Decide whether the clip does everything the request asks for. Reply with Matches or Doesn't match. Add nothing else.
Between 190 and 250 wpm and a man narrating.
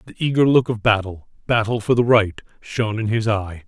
Doesn't match